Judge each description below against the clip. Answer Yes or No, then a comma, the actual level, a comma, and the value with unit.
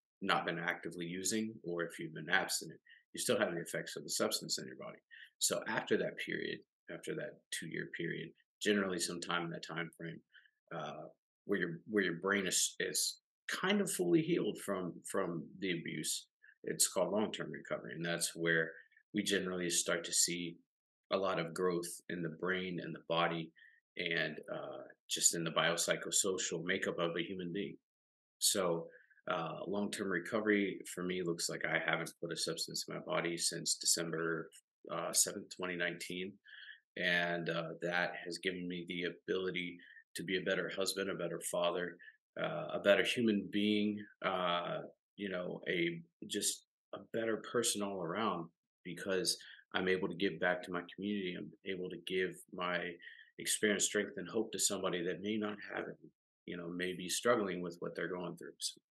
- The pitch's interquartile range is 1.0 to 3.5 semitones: Yes, average, 2.9 semitones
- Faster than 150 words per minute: Yes, average, 175 wpm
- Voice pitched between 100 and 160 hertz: No, very low, 90 Hz